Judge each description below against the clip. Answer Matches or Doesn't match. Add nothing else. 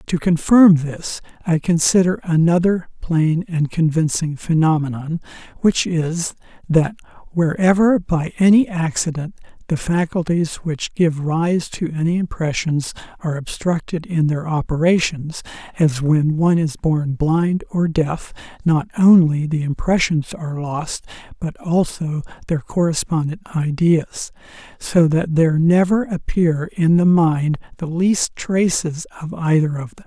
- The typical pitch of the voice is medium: Matches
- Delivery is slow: Matches